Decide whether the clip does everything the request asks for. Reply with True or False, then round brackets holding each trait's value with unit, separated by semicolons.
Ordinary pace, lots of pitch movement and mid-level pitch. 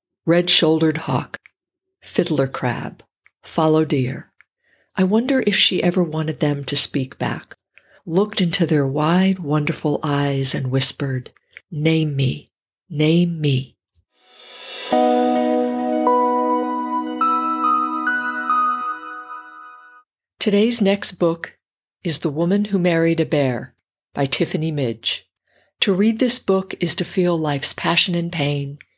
False (110 wpm; 6.3 semitones; 165 Hz)